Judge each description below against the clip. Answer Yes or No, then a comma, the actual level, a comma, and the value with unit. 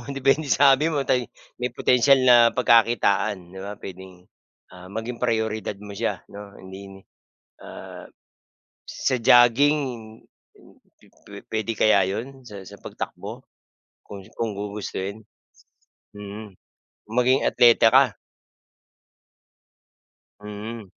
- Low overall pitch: Yes, low, 110 Hz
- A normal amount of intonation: Yes, average, 3.8 semitones